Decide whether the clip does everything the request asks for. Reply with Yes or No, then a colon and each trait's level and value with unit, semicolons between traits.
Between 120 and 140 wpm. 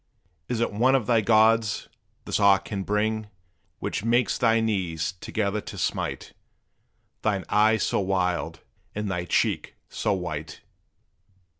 Yes: slow, 135 wpm